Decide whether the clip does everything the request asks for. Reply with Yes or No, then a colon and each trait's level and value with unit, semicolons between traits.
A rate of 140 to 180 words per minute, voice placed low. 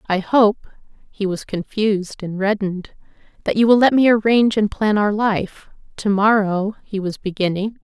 No: average, 145 wpm; high, 205 Hz